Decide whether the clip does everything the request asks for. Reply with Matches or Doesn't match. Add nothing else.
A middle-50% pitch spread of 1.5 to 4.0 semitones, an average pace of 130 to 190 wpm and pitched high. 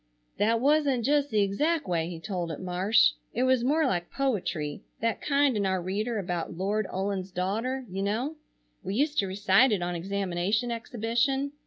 Doesn't match